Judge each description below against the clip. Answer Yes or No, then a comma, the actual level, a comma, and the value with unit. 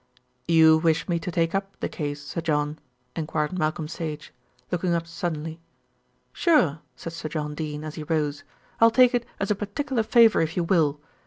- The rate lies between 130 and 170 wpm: No, average, 180 wpm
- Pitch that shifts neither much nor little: Yes, average, 3.3 semitones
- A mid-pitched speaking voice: Yes, medium, 165 Hz